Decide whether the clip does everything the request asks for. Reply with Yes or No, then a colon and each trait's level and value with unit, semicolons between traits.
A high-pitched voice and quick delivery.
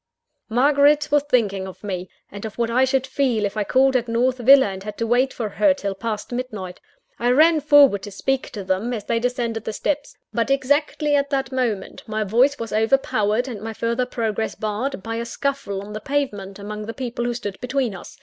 Yes: high, 235 Hz; fast, 215 wpm